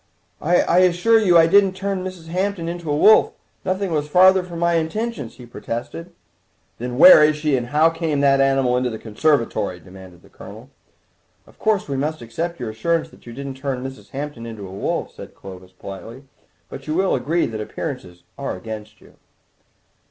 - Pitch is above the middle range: No, medium, 145 Hz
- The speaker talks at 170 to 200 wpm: Yes, average, 185 wpm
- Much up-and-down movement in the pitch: Yes, wide, 6.6 semitones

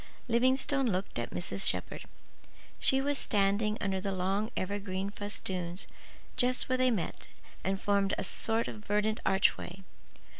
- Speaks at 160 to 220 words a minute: No, average, 140 wpm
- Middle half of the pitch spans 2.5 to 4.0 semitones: Yes, average, 3.1 semitones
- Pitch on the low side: No, high, 200 Hz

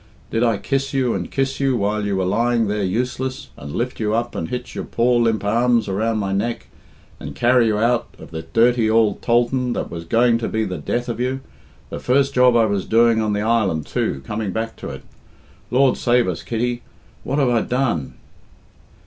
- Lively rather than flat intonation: No, average, 2.9 semitones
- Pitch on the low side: Yes, low, 115 Hz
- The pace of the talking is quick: Yes, fast, 210 wpm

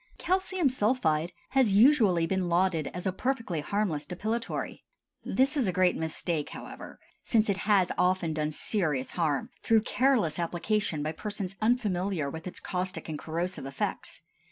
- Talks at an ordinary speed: Yes, average, 150 wpm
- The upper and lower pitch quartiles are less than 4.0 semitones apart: No, average, 5.0 semitones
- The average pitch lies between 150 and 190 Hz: Yes, medium, 185 Hz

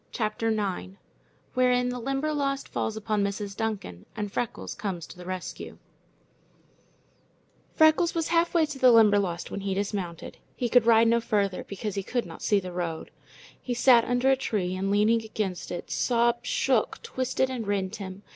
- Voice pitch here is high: Yes, high, 220 Hz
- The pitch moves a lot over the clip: No, average, 4.1 semitones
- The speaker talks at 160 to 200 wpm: Yes, average, 165 wpm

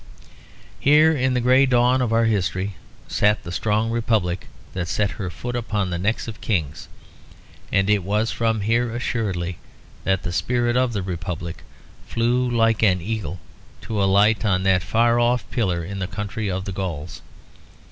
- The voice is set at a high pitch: No, low, 105 Hz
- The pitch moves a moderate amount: Yes, average, 4.1 semitones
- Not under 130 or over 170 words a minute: Yes, average, 165 wpm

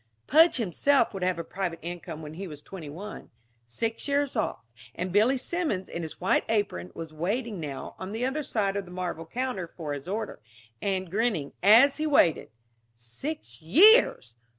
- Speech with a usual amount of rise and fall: No, wide, 6.7 semitones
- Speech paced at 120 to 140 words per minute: No, average, 175 wpm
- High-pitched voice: Yes, high, 195 Hz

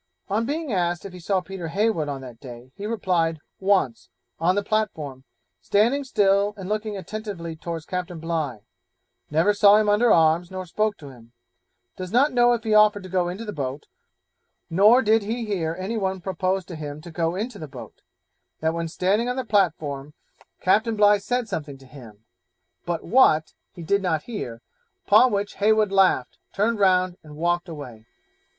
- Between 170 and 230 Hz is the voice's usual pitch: Yes, medium, 185 Hz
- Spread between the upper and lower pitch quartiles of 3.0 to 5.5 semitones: Yes, average, 4.7 semitones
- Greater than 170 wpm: Yes, average, 180 wpm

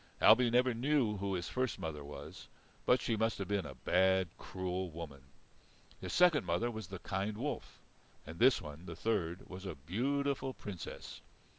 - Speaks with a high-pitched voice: No, low, 100 Hz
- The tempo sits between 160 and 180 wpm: Yes, average, 170 wpm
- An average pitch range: No, wide, 5.7 semitones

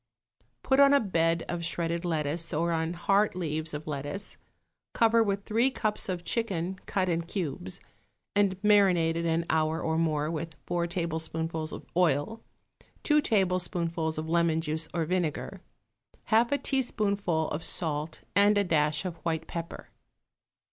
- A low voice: No, medium, 170 Hz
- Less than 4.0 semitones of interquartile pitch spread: Yes, average, 3.6 semitones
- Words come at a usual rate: Yes, average, 150 wpm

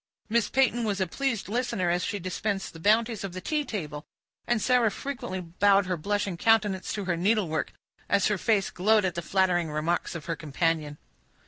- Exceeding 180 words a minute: Yes, average, 190 wpm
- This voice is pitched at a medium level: No, high, 195 Hz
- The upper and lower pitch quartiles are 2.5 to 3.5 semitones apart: No, average, 4.2 semitones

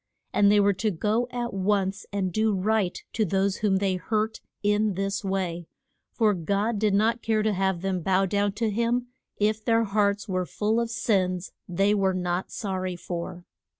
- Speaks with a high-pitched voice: Yes, high, 200 Hz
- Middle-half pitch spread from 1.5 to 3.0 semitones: Yes, narrow, 2.4 semitones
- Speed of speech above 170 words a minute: Yes, average, 185 wpm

